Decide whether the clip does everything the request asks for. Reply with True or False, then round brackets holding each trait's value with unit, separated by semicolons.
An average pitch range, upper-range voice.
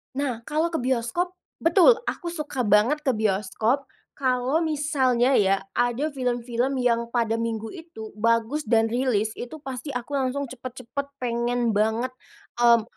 True (3.5 semitones; 250 Hz)